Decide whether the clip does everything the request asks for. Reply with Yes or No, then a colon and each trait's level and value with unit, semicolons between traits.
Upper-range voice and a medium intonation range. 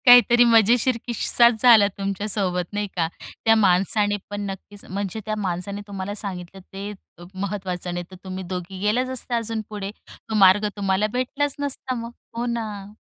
Yes: high, 205 Hz; average, 3.2 semitones